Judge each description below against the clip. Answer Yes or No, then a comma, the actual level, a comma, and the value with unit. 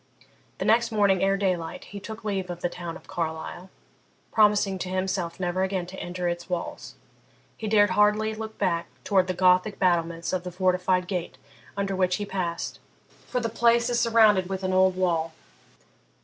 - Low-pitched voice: No, medium, 185 Hz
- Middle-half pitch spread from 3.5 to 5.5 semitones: No, narrow, 2.6 semitones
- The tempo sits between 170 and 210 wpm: Yes, average, 175 wpm